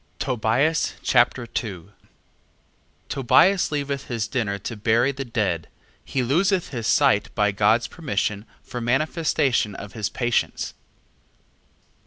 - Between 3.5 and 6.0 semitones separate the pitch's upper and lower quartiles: Yes, average, 4.6 semitones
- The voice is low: Yes, low, 120 Hz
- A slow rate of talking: Yes, slow, 115 wpm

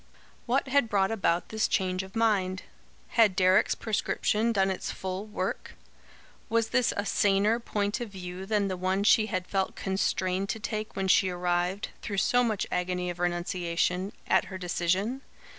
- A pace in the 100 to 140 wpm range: No, average, 165 wpm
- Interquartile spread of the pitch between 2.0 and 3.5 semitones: Yes, average, 2.8 semitones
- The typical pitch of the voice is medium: No, high, 195 Hz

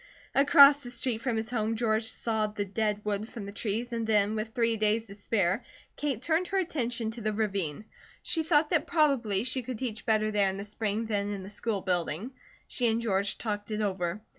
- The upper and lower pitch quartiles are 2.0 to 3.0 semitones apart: Yes, average, 2.7 semitones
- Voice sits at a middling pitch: No, high, 220 Hz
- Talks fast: Yes, fast, 215 wpm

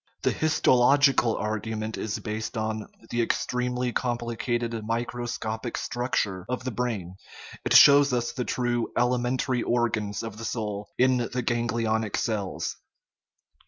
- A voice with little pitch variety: Yes, narrow, 2.2 semitones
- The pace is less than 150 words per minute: Yes, slow, 135 wpm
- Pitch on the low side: Yes, low, 120 Hz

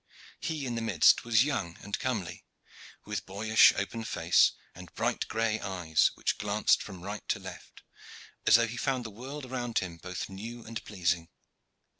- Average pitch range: Yes, average, 4.2 semitones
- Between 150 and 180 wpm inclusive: Yes, average, 170 wpm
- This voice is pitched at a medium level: No, low, 110 Hz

